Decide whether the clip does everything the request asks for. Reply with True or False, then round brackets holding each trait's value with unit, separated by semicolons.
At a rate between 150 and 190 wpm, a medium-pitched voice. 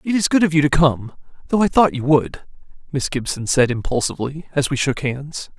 False (205 wpm; 145 Hz)